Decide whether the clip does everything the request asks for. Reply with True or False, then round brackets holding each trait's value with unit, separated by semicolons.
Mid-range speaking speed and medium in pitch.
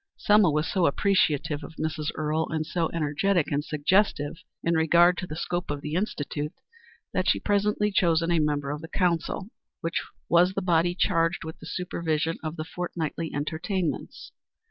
True (170 wpm; 165 Hz)